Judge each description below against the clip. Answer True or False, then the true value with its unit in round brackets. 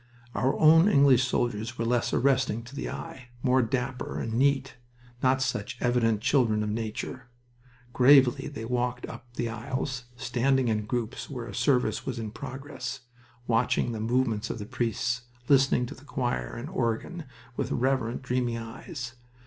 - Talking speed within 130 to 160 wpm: True (155 wpm)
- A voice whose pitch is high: False (125 Hz)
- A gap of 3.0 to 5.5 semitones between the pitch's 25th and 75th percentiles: False (2.4 semitones)